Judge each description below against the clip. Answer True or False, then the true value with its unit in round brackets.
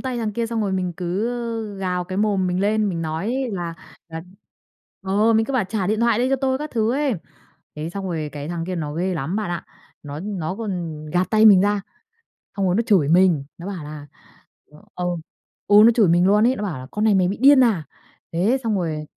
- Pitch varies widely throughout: False (4.3 semitones)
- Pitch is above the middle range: True (195 Hz)